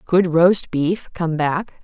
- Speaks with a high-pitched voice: No, medium, 170 Hz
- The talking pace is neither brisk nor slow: Yes, average, 165 wpm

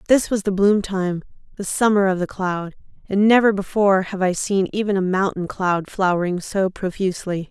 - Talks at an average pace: Yes, average, 185 wpm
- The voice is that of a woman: Yes, female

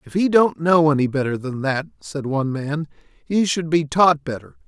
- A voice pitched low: No, medium, 150 Hz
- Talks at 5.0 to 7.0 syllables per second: No, 4.8 syllables/s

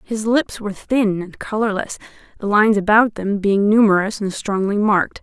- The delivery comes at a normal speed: Yes, average, 170 wpm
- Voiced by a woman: Yes, female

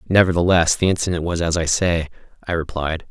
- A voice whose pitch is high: No, very low, 85 Hz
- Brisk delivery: No, average, 175 wpm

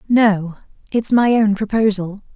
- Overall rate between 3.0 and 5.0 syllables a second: Yes, 4.0 syllables/s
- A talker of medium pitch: No, high, 210 Hz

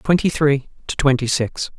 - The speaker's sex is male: Yes, male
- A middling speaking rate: Yes, average, 170 wpm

